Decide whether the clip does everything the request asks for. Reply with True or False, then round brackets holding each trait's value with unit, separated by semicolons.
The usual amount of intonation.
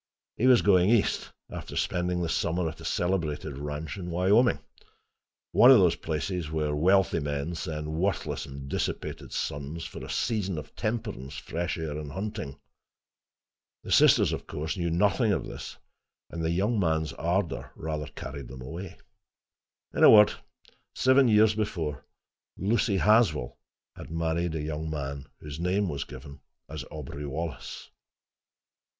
True (4.3 semitones)